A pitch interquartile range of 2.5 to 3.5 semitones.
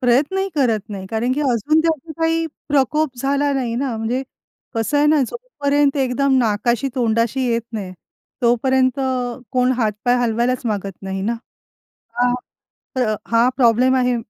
Yes: average, 3.2 semitones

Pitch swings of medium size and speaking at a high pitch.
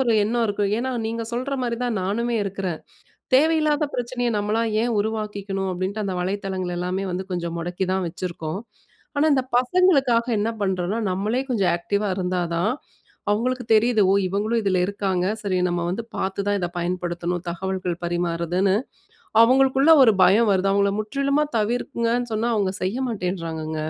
Yes: average, 4.3 semitones; high, 200 Hz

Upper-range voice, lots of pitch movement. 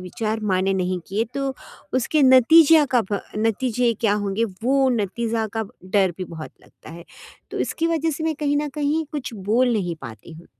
Yes: high, 225 Hz; wide, 6.4 semitones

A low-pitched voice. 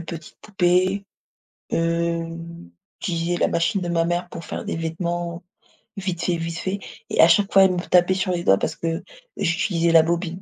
No: medium, 170 Hz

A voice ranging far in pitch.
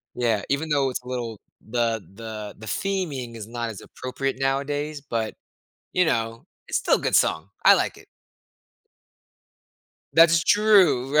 No: average, 4.6 semitones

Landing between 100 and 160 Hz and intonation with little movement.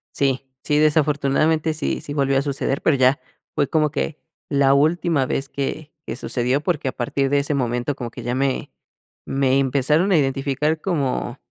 Yes: medium, 140 Hz; narrow, 2.2 semitones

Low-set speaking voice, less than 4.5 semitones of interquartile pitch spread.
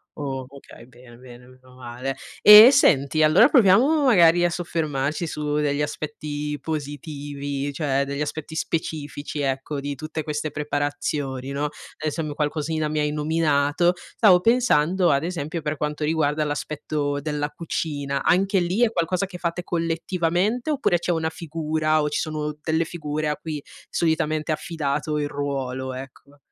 No: medium, 150 Hz; narrow, 2.5 semitones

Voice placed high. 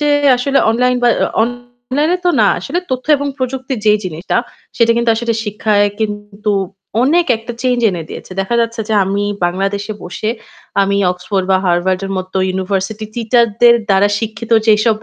Yes: high, 220 Hz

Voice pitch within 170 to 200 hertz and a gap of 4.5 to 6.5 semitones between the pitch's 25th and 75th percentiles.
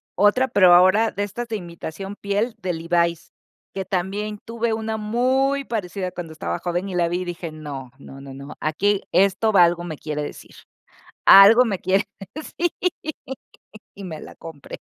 No: high, 190 Hz; average, 4.0 semitones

